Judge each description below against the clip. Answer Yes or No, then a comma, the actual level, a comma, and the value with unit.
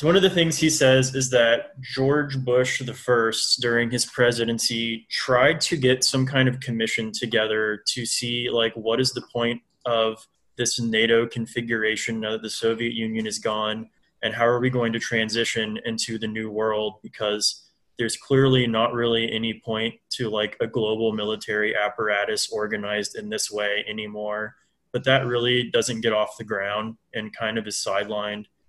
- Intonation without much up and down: Yes, narrow, 2.1 semitones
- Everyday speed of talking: Yes, average, 175 wpm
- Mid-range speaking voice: No, low, 115 Hz